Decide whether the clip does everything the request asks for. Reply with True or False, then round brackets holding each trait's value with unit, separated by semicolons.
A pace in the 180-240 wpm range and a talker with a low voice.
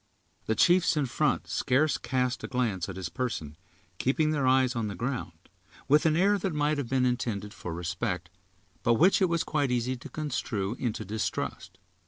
True (185 wpm; 125 Hz)